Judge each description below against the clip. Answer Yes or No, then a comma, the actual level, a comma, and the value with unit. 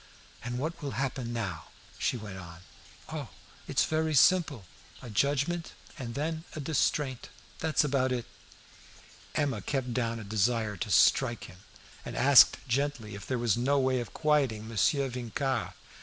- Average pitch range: Yes, average, 3.8 semitones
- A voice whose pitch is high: No, low, 130 Hz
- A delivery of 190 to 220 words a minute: No, average, 155 wpm